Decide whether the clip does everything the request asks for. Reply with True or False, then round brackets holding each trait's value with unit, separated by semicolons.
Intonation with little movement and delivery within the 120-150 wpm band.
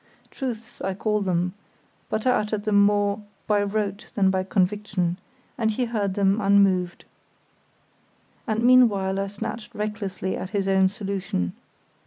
True (2.0 semitones; 140 wpm)